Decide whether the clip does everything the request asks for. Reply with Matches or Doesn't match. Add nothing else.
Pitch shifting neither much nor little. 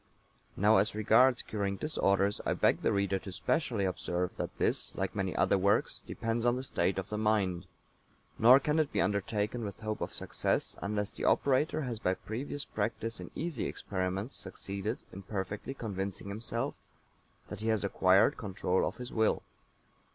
Matches